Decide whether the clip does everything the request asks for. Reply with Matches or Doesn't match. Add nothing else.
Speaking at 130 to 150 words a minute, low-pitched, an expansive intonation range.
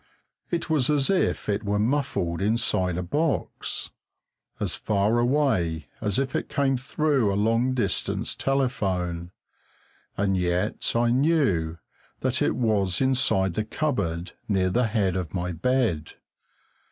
Matches